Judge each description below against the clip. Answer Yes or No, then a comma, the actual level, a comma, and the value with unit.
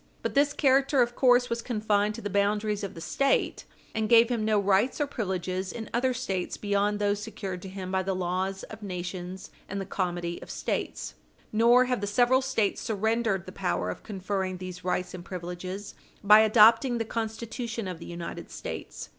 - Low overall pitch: No, high, 205 Hz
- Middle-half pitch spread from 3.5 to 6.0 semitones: Yes, average, 3.8 semitones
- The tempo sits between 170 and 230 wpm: Yes, average, 190 wpm